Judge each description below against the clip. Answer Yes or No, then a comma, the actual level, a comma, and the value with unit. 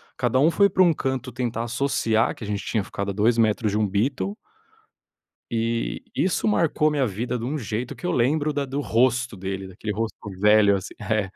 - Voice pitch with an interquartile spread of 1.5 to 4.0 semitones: No, average, 4.4 semitones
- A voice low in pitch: Yes, low, 115 Hz